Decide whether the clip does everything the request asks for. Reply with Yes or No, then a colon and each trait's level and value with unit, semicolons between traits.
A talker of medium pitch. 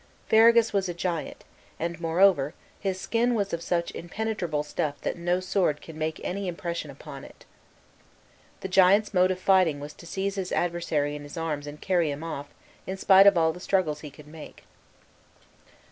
Yes: medium, 175 Hz